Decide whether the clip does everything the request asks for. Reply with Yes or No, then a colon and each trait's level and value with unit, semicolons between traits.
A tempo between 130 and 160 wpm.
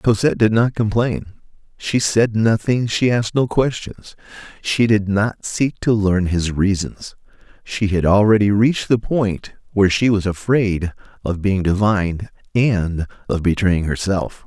Yes: average, 150 wpm